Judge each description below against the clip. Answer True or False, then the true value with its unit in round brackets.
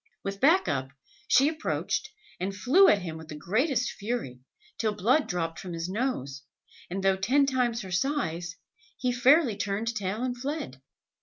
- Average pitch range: False (6.4 semitones)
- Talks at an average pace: True (165 wpm)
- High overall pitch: True (210 Hz)